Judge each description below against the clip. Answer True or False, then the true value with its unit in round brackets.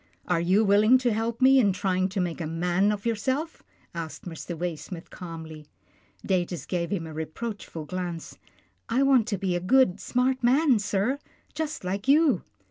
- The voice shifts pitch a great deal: True (5.8 semitones)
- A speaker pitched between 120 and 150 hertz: False (195 Hz)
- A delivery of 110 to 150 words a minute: False (180 wpm)